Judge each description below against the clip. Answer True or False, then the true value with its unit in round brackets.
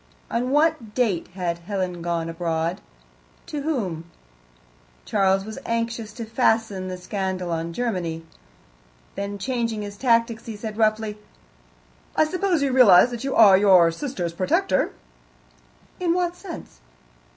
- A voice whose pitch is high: True (210 Hz)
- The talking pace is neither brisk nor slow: False (130 wpm)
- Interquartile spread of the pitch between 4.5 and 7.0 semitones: True (5.1 semitones)